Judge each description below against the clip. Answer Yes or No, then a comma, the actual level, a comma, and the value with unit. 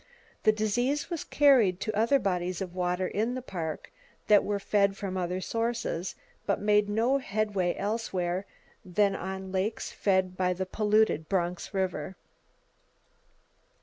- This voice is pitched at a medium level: No, high, 195 Hz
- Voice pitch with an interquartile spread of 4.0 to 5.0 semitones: No, average, 2.9 semitones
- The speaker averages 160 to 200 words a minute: No, average, 140 wpm